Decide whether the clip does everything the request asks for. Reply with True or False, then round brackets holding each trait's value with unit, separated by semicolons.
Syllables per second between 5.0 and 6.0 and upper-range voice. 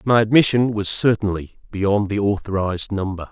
False (5.2 syllables/s; 105 Hz)